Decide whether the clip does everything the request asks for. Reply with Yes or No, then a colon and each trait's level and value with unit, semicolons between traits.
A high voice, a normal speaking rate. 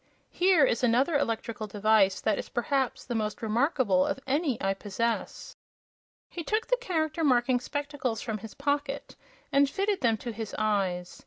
Yes: high, 245 Hz; average, 160 wpm